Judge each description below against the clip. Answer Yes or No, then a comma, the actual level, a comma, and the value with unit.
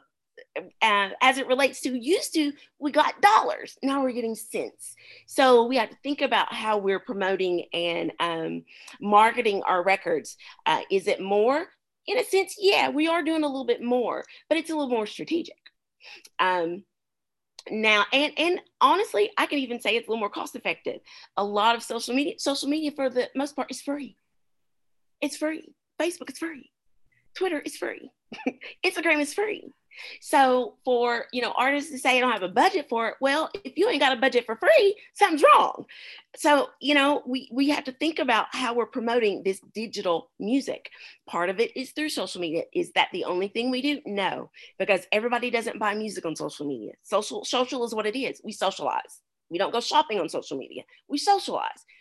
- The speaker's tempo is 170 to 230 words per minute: Yes, average, 195 wpm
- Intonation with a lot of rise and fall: Yes, wide, 6.0 semitones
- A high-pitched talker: Yes, very high, 265 Hz